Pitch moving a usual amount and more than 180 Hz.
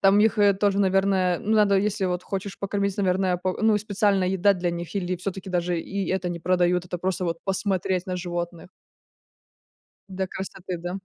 No: narrow, 1.9 semitones; high, 190 Hz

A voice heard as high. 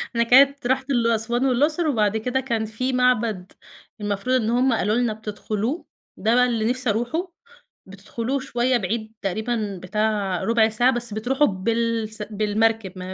Yes: high, 230 Hz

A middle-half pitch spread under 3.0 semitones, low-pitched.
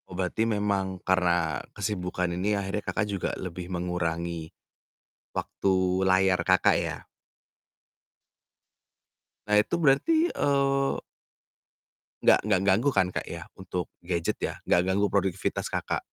Yes: narrow, 2.4 semitones; very low, 95 Hz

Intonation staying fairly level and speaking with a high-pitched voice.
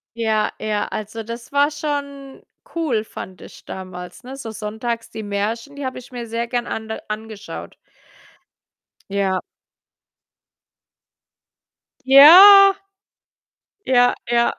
No: average, 4.2 semitones; high, 235 Hz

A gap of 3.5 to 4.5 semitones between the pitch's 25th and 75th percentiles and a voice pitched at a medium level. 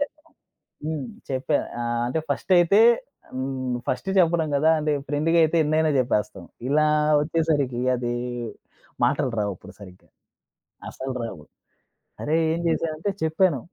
Yes: average, 4.1 semitones; medium, 150 Hz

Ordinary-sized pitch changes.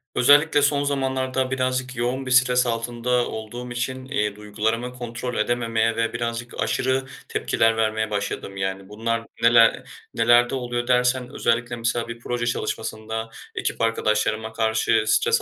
No: narrow, 2.0 semitones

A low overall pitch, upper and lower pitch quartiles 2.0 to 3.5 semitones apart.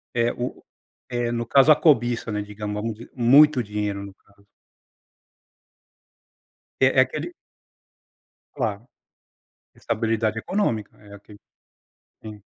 Yes: low, 110 Hz; narrow, 2.6 semitones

